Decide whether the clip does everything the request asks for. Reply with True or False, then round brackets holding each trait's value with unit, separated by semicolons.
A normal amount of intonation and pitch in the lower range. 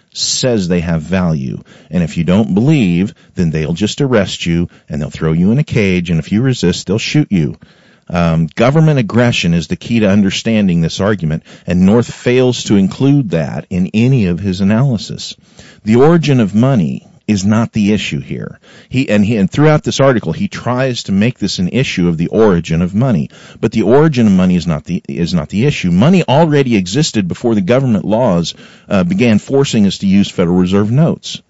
False (7.7 semitones; 115 Hz)